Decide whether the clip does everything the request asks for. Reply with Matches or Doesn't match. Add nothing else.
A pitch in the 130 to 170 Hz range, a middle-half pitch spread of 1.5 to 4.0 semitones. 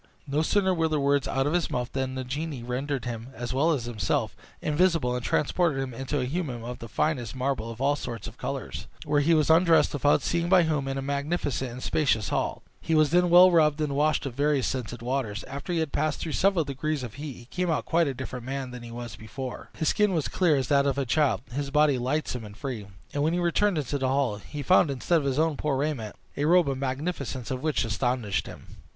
Matches